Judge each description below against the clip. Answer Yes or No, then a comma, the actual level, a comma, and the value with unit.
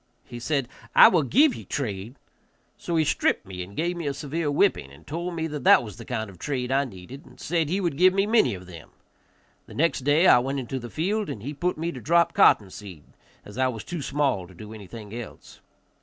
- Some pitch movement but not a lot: No, wide, 7.2 semitones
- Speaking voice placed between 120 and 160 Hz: Yes, low, 135 Hz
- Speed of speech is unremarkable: No, fast, 235 wpm